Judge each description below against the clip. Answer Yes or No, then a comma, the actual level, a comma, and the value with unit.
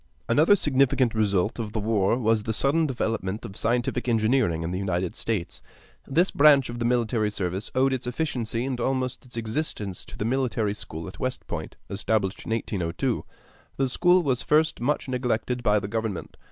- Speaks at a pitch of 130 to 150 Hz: No, low, 115 Hz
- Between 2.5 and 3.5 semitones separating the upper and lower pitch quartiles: No, average, 3.9 semitones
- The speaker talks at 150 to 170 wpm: No, average, 180 wpm